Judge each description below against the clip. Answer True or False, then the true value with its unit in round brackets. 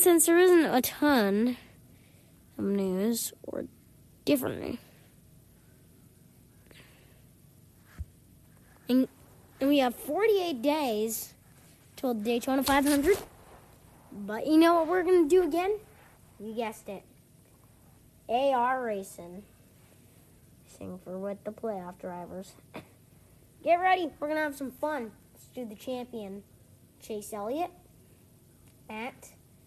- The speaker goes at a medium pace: False (100 wpm)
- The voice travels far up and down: True (6.4 semitones)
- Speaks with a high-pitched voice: True (255 Hz)